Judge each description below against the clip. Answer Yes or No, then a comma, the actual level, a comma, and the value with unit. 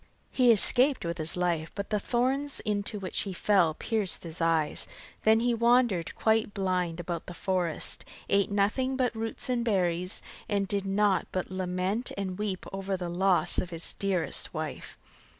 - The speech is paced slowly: No, average, 170 wpm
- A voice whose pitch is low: No, high, 195 Hz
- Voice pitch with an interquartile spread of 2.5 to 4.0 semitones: Yes, average, 3.7 semitones